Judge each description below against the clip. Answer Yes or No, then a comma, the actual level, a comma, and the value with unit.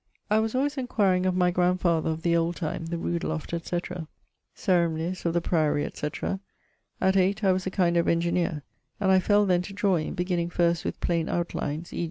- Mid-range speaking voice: Yes, medium, 175 Hz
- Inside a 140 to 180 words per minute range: No, average, 200 wpm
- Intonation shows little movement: Yes, narrow, 2.0 semitones